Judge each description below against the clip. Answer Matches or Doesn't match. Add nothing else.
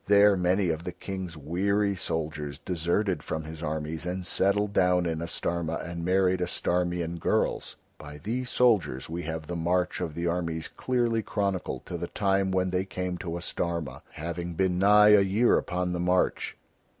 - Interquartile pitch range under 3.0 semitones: Matches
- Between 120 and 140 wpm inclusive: Doesn't match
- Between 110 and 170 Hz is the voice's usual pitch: Doesn't match